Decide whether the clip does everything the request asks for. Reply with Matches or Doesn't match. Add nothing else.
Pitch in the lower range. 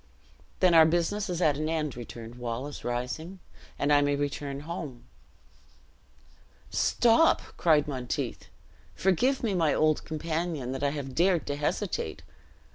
Doesn't match